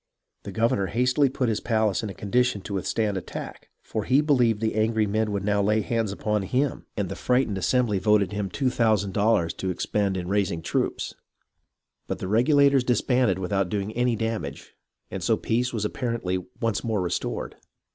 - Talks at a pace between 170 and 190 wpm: Yes, average, 185 wpm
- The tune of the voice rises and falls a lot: No, average, 3.5 semitones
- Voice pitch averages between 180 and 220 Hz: No, low, 110 Hz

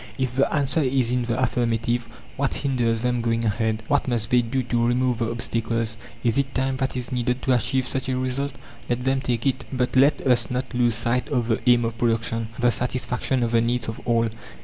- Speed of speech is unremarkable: No, fast, 215 wpm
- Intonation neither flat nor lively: No, narrow, 1.9 semitones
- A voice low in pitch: Yes, low, 125 Hz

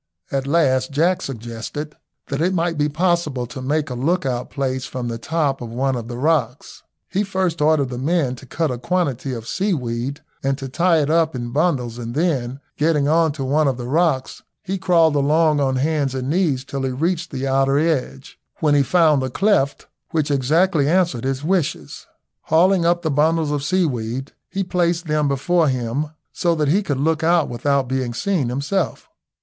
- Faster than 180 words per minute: Yes, average, 190 wpm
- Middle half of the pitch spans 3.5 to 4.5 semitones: Yes, average, 4.2 semitones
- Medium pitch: Yes, medium, 145 Hz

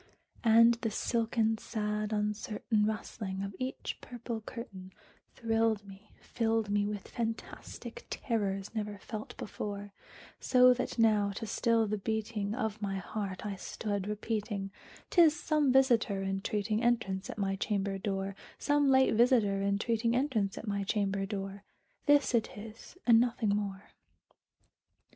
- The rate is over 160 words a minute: No, average, 140 wpm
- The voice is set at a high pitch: Yes, high, 215 Hz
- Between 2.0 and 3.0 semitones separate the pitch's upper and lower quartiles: Yes, narrow, 2.5 semitones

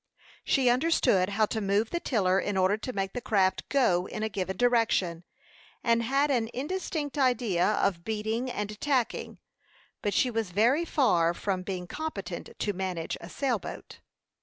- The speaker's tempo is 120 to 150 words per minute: No, average, 160 wpm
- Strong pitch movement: No, average, 4.8 semitones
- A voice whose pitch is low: No, high, 215 Hz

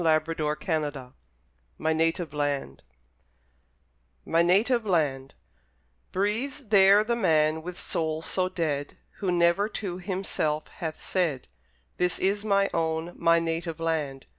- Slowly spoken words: Yes, slow, 110 wpm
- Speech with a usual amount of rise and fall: Yes, average, 3.9 semitones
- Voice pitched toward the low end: No, medium, 165 Hz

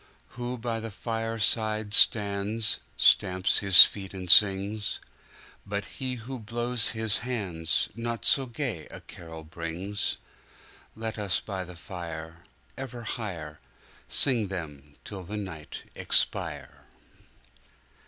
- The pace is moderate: No, slow, 110 wpm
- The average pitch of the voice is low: Yes, low, 105 Hz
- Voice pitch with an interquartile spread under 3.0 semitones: No, average, 4.0 semitones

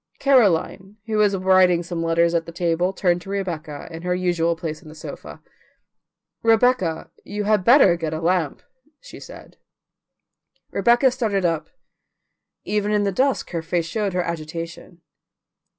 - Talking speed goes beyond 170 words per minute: No, average, 150 wpm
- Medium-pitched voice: Yes, medium, 180 Hz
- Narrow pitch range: No, average, 3.7 semitones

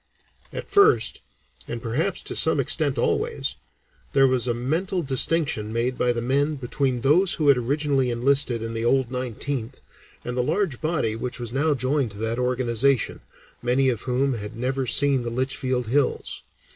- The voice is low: Yes, low, 130 Hz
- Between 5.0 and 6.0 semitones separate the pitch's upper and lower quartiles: No, average, 2.8 semitones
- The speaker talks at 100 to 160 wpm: No, average, 170 wpm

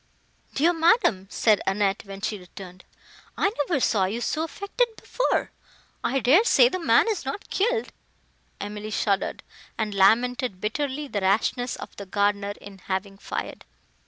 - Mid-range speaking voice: No, high, 220 Hz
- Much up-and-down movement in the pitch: Yes, wide, 7.4 semitones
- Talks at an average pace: Yes, average, 150 wpm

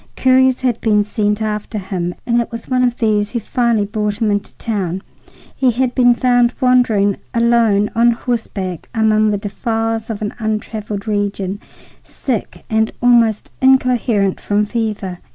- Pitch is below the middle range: No, high, 220 Hz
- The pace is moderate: Yes, average, 155 wpm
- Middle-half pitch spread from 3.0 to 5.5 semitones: No, narrow, 2.6 semitones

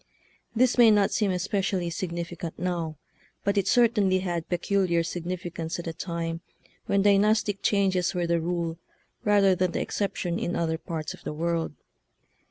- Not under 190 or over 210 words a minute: No, average, 160 wpm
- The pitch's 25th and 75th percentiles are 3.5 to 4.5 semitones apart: No, average, 2.8 semitones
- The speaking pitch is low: No, medium, 180 Hz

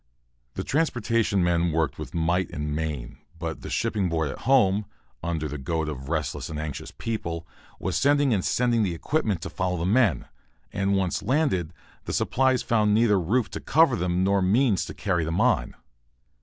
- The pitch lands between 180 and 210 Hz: No, very low, 90 Hz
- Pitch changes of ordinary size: No, wide, 5.9 semitones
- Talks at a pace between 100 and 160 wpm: No, average, 180 wpm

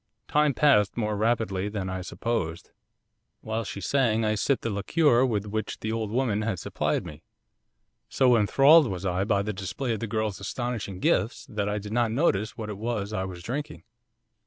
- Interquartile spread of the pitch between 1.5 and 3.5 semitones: Yes, average, 3.1 semitones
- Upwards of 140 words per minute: Yes, average, 185 wpm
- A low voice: Yes, low, 110 Hz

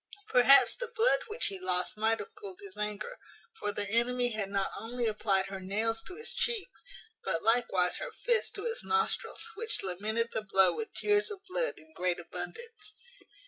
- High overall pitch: Yes, high, 235 Hz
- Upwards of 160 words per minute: Yes, average, 185 wpm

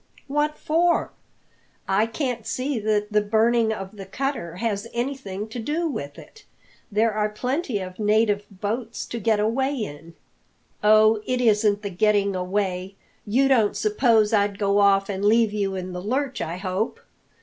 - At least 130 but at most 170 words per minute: Yes, average, 160 wpm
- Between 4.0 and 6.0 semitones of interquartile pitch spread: No, average, 3.0 semitones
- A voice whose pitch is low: No, high, 215 Hz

